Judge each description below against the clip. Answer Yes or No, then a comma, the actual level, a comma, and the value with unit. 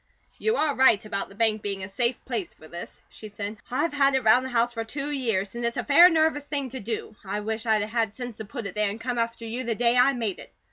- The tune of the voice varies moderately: Yes, average, 3.6 semitones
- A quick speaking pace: Yes, fast, 280 wpm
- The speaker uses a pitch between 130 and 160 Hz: No, high, 230 Hz